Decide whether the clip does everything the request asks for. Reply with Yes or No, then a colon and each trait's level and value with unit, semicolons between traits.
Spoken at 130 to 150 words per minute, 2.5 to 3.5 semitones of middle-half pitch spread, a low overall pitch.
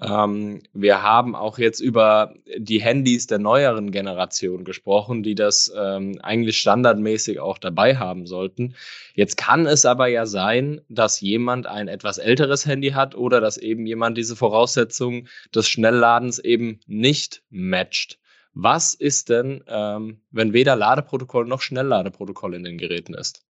Yes: average, 140 wpm; average, 3.1 semitones; low, 110 Hz